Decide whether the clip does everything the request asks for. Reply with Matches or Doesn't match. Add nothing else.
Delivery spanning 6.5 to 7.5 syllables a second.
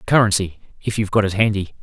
Matches